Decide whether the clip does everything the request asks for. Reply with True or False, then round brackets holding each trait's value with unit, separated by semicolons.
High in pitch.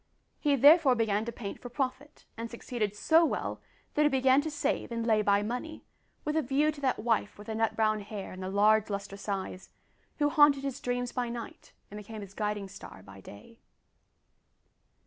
True (230 Hz)